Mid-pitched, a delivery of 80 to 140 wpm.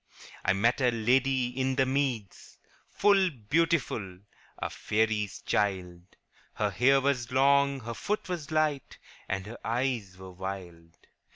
No: low, 120 Hz; slow, 135 wpm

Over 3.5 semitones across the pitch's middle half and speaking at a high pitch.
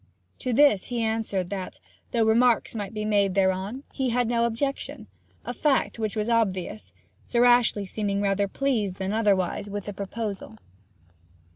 No: average, 3.1 semitones; high, 215 Hz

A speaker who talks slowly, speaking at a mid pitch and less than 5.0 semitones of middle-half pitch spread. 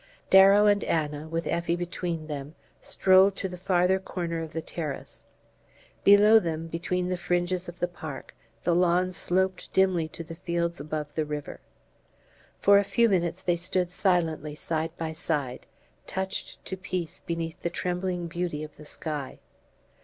No: average, 160 wpm; medium, 175 Hz; narrow, 2.4 semitones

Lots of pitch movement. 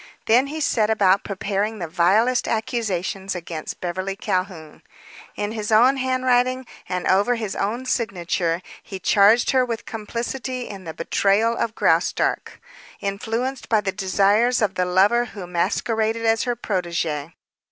No: average, 4.1 semitones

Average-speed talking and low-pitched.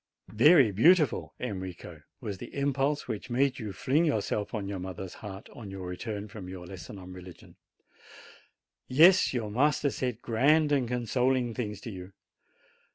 Yes: average, 155 wpm; low, 110 Hz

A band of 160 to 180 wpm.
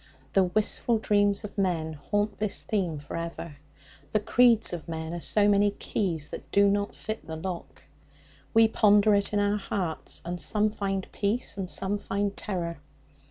Yes: average, 170 wpm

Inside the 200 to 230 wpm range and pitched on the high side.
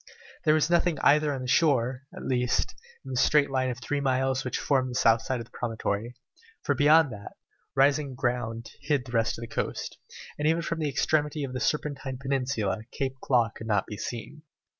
No: fast, 205 wpm; low, 130 Hz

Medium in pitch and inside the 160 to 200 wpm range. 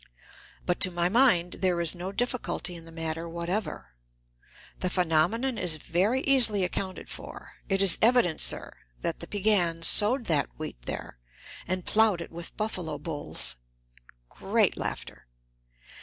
No: medium, 180 Hz; average, 140 wpm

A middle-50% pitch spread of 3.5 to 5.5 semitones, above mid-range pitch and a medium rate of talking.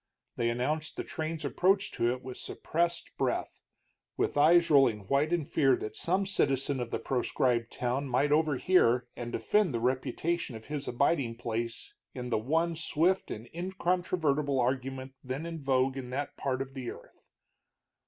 No: average, 4.6 semitones; low, 135 Hz; average, 165 wpm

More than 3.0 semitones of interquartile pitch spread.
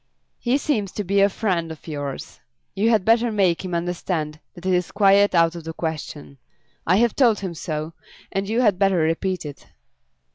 Yes: average, 3.8 semitones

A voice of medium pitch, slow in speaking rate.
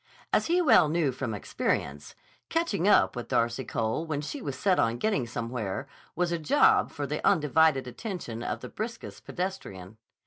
No: medium, 150 Hz; average, 170 wpm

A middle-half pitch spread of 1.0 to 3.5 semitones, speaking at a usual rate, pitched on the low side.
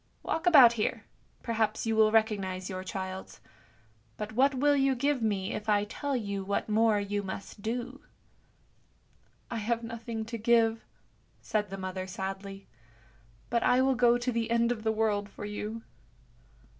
No: average, 2.7 semitones; average, 170 wpm; high, 220 Hz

